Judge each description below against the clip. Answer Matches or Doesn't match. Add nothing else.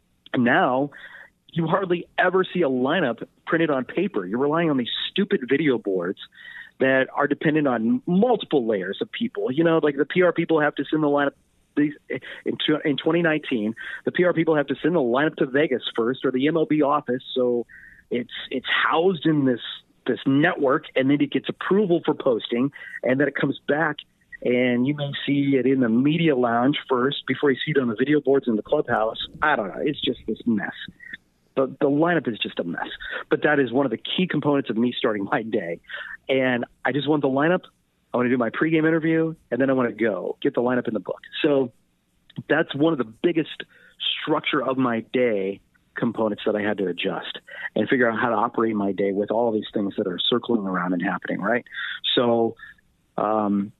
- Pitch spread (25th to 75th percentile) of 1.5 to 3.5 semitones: Doesn't match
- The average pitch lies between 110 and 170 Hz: Matches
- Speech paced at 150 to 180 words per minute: Doesn't match